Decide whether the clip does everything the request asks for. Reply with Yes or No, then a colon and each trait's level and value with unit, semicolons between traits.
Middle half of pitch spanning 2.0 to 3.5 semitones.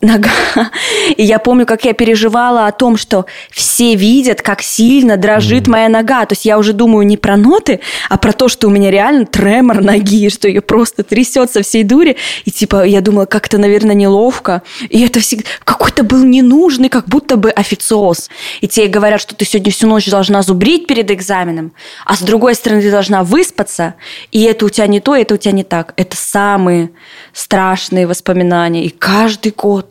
Yes: average, 2.8 semitones